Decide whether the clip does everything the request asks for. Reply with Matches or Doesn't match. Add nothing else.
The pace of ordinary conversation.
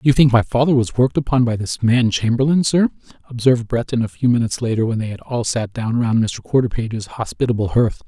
Doesn't match